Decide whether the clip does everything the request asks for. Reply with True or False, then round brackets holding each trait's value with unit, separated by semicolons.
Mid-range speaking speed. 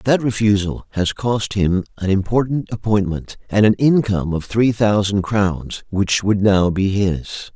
True (160 wpm)